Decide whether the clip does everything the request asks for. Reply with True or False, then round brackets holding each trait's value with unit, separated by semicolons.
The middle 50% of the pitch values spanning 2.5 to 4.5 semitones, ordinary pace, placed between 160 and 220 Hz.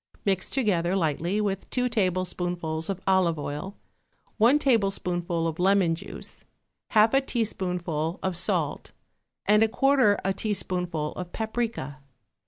False (3.7 semitones; 125 wpm; 190 Hz)